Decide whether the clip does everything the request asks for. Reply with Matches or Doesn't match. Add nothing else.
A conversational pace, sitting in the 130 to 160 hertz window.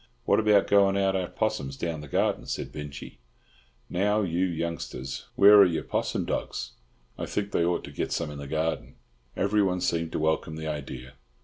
Doesn't match